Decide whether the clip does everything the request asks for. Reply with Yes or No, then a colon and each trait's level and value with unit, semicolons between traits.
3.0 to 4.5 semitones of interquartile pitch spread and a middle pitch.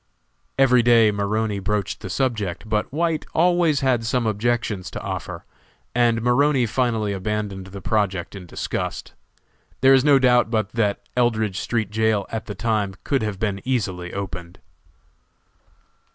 No: average, 3.4 semitones; low, 110 Hz